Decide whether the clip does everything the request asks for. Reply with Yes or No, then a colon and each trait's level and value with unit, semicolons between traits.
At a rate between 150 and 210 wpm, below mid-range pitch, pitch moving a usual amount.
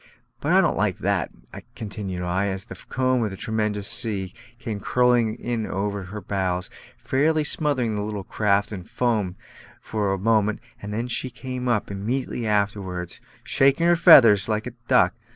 Yes: average, 165 wpm; low, 105 Hz; average, 3.7 semitones